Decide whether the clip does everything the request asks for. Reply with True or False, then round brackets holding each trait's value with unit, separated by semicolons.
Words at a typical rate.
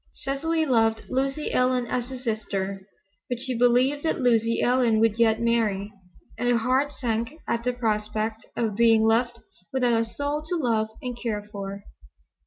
True (165 wpm)